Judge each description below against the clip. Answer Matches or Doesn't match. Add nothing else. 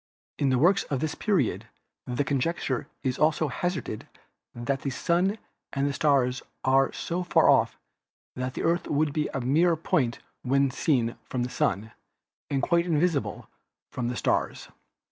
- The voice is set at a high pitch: Doesn't match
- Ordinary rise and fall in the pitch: Matches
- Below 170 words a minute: Matches